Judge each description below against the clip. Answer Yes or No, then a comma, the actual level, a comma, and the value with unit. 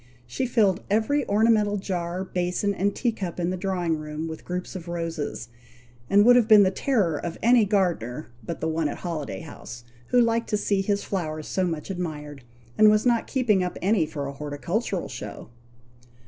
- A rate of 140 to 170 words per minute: No, average, 190 wpm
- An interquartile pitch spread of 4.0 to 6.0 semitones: Yes, average, 4.6 semitones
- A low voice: No, medium, 185 Hz